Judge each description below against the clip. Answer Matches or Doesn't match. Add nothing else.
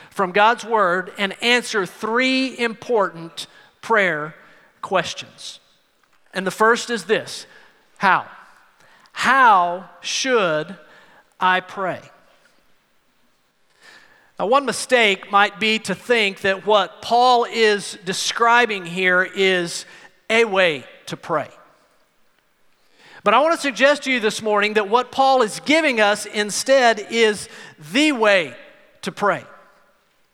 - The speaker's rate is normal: Doesn't match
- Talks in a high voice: Matches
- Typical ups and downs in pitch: Matches